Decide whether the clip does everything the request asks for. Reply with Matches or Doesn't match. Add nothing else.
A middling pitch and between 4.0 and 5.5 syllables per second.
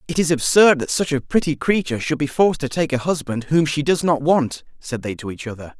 Doesn't match